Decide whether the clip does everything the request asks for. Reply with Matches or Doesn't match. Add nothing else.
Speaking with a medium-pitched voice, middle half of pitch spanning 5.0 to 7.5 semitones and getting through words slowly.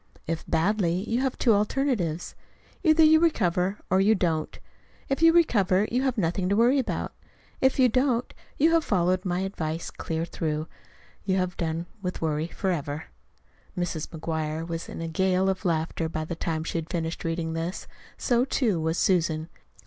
Doesn't match